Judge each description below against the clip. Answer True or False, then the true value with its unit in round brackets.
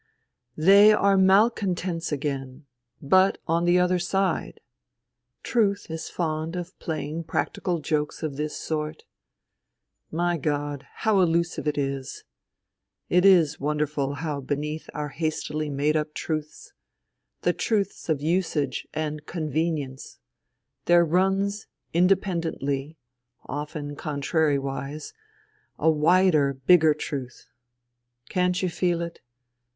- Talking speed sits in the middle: False (115 wpm)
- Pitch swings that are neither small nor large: True (3.4 semitones)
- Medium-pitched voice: True (155 Hz)